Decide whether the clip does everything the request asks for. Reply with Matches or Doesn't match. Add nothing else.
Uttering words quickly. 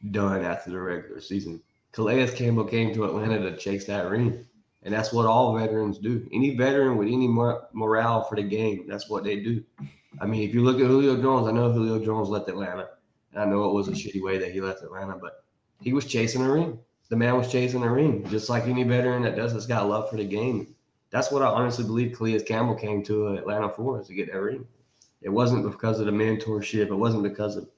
Matches